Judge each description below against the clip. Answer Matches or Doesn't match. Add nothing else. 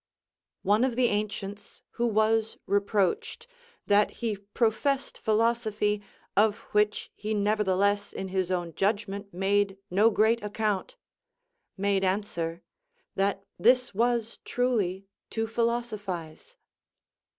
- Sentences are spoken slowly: Matches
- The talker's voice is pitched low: Doesn't match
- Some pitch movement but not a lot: Doesn't match